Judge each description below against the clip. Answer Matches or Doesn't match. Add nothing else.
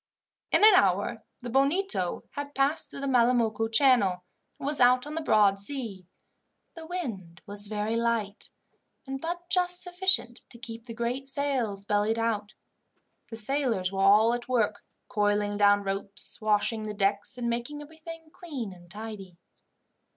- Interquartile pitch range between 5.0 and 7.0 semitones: Matches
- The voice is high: Matches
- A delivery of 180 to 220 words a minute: Doesn't match